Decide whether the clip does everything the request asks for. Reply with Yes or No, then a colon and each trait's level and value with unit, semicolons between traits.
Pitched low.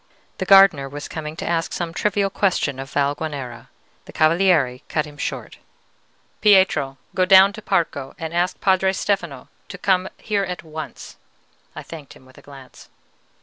No: medium, 165 Hz